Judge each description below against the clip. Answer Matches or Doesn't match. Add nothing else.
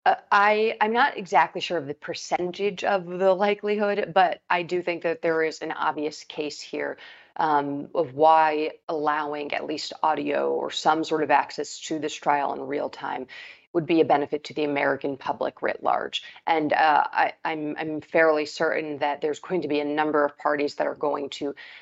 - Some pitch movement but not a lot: Matches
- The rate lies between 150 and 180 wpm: Doesn't match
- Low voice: Doesn't match